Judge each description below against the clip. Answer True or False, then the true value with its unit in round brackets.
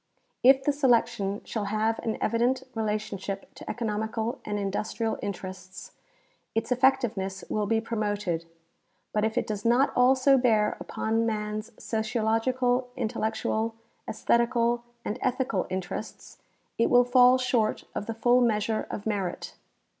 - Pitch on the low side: False (225 Hz)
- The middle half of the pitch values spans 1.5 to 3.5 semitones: True (2.7 semitones)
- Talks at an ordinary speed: False (130 wpm)